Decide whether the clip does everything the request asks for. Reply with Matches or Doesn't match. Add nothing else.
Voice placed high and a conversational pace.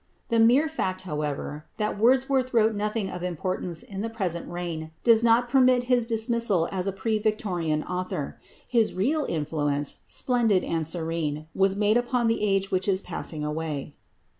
Matches